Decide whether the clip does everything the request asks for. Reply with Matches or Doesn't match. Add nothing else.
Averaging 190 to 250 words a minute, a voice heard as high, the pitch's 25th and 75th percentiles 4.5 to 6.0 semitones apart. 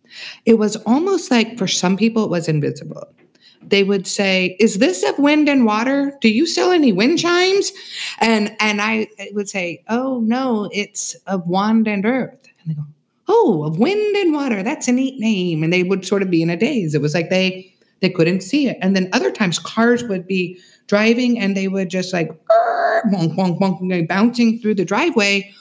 Matches